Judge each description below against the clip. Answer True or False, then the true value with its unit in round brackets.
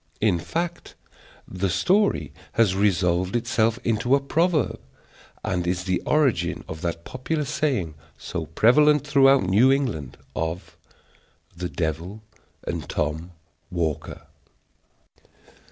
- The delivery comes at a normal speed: False (115 wpm)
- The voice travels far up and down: True (7.8 semitones)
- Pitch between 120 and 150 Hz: False (105 Hz)